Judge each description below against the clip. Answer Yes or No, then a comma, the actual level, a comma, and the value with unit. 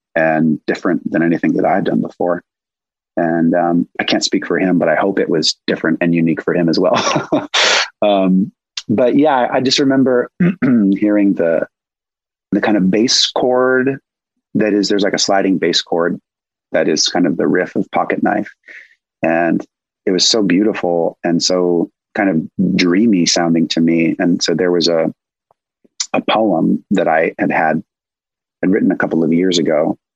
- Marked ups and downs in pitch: Yes, wide, 7.1 semitones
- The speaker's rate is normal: Yes, average, 175 wpm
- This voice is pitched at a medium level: No, very low, 90 Hz